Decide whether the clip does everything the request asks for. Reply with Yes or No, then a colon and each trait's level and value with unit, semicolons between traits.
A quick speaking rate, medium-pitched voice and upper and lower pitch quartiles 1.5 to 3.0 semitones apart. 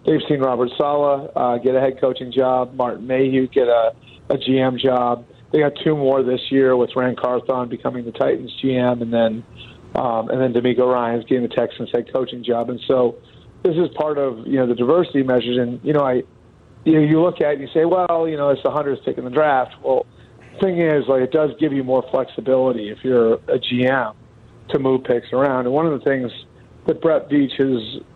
No: fast, 220 wpm; low, 130 Hz; narrow, 2.4 semitones